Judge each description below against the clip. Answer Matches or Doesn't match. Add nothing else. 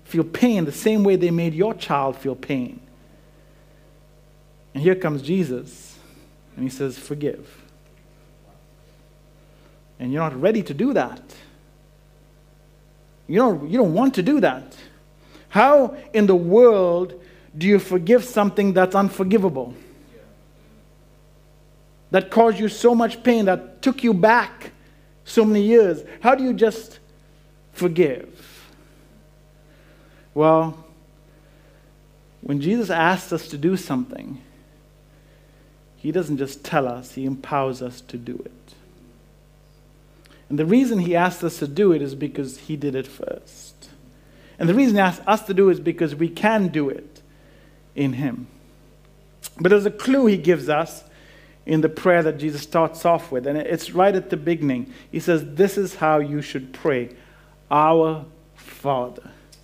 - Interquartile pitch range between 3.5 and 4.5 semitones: Matches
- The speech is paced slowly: Doesn't match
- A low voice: Doesn't match